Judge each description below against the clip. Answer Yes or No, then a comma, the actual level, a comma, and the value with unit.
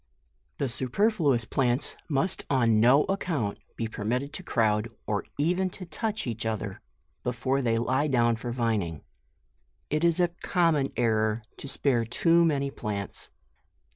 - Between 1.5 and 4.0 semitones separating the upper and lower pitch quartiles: No, average, 5.3 semitones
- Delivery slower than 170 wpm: Yes, average, 140 wpm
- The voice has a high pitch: No, low, 125 Hz